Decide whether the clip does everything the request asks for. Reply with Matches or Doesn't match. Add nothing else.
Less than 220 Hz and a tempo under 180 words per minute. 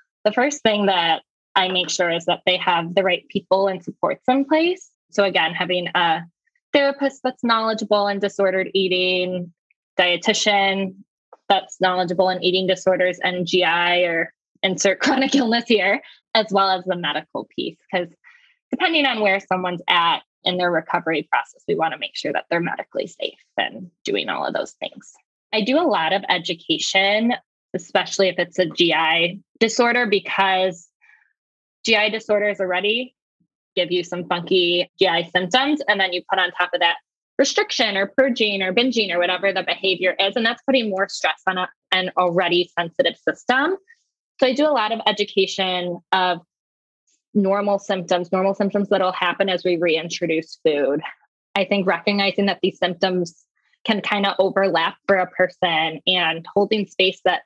Matches